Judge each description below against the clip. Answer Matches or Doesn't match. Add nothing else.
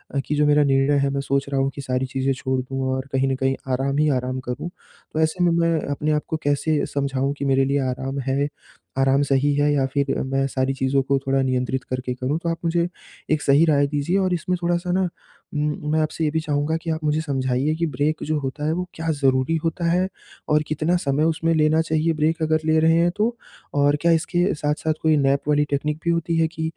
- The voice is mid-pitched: Matches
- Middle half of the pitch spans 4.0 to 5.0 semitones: Doesn't match